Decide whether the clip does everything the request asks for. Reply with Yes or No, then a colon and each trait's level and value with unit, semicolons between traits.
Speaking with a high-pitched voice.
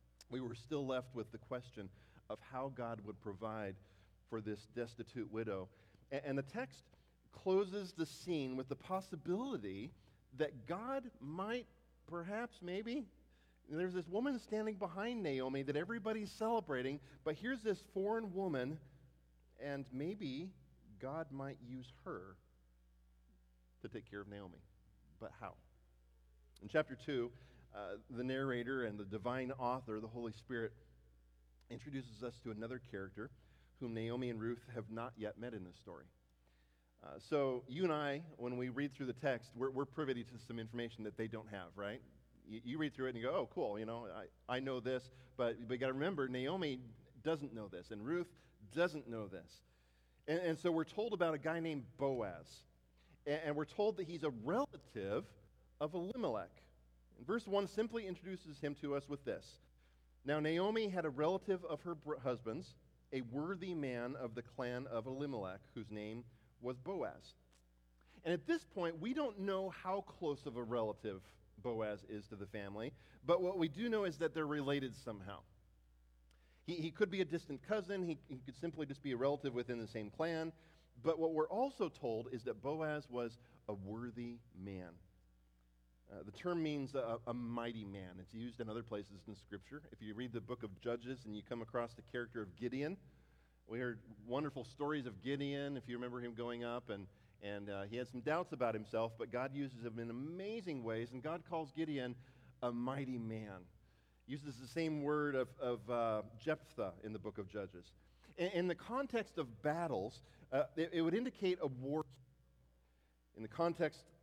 No: low, 125 Hz